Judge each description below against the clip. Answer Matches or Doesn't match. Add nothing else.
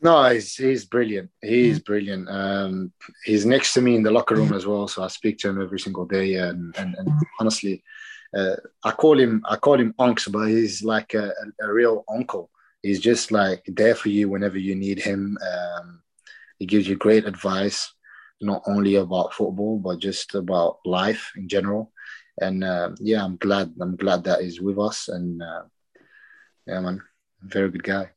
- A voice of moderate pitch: Doesn't match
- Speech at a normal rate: Matches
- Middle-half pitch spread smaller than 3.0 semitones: Matches